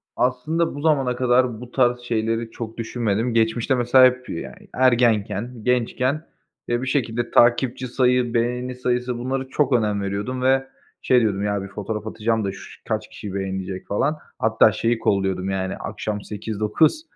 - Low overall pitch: Yes, low, 120 Hz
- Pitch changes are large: No, average, 3.0 semitones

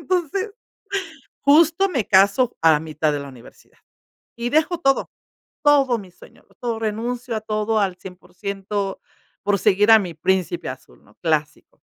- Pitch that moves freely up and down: Yes, wide, 6.2 semitones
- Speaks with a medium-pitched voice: No, high, 215 Hz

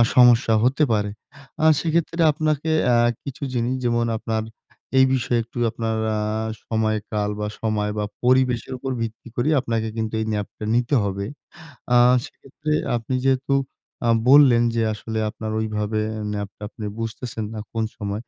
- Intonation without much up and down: No, average, 3.1 semitones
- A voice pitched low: Yes, low, 115 Hz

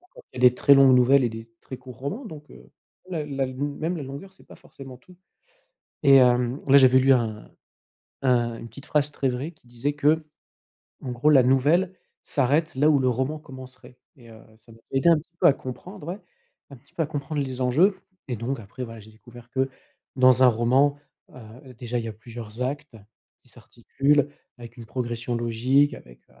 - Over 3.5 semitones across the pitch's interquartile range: No, average, 3.2 semitones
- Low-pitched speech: Yes, low, 130 Hz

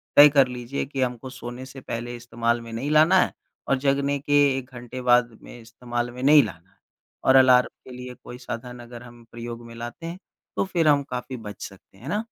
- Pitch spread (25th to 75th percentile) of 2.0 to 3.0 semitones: Yes, narrow, 2.5 semitones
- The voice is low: Yes, low, 125 Hz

